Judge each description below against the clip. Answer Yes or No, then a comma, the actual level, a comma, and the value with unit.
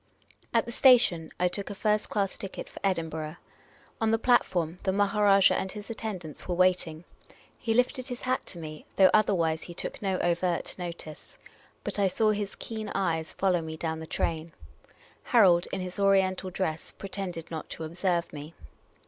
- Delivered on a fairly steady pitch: No, average, 3.7 semitones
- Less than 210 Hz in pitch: Yes, medium, 185 Hz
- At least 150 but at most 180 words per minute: Yes, average, 175 wpm